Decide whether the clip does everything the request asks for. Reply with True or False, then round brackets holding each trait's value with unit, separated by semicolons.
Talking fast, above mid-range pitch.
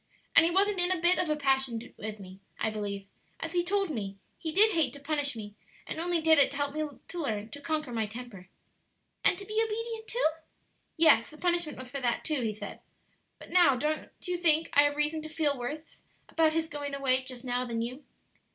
True (225 wpm; 295 Hz)